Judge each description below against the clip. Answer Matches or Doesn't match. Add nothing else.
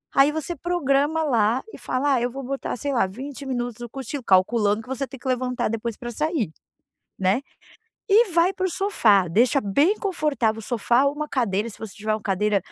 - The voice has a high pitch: Matches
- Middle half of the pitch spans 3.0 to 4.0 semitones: Doesn't match